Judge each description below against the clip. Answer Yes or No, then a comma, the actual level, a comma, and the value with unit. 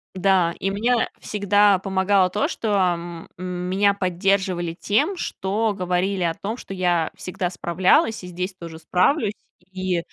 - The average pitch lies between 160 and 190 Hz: Yes, medium, 185 Hz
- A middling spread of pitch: No, narrow, 2.1 semitones